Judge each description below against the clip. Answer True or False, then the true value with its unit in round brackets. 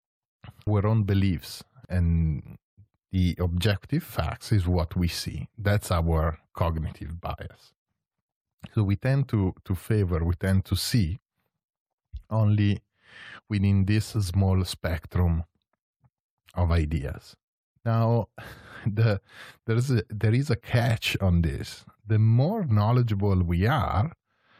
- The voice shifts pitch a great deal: False (3.9 semitones)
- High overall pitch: False (100 Hz)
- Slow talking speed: True (115 wpm)